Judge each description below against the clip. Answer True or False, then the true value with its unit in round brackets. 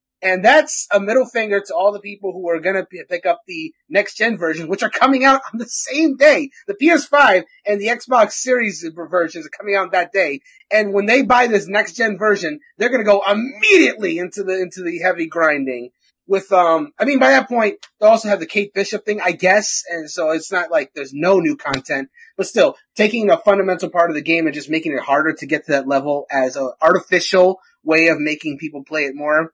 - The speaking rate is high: True (220 wpm)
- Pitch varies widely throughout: True (6.9 semitones)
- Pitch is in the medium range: False (200 Hz)